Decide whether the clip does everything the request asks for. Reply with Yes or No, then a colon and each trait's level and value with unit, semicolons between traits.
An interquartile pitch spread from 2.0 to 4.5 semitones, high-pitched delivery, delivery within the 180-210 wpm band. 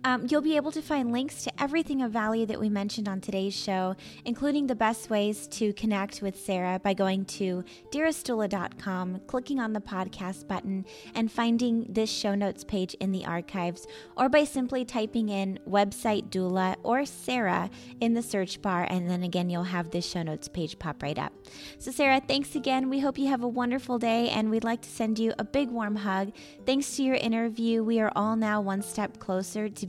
Yes: average, 4.2 semitones; high, 215 Hz; fast, 205 wpm